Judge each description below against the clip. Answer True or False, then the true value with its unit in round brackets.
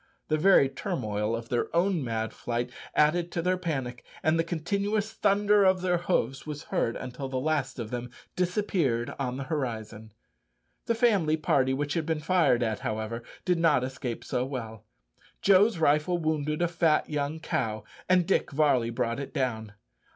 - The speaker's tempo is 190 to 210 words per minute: False (170 wpm)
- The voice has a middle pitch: True (150 Hz)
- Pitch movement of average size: False (6.0 semitones)